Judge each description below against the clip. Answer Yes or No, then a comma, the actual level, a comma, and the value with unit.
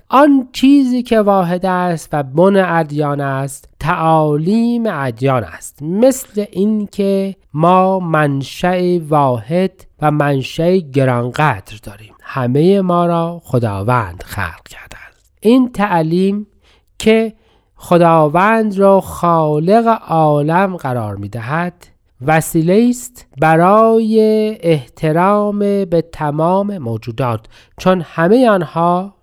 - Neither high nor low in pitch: Yes, medium, 170 Hz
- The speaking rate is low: Yes, slow, 95 wpm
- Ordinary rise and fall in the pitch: No, wide, 6.1 semitones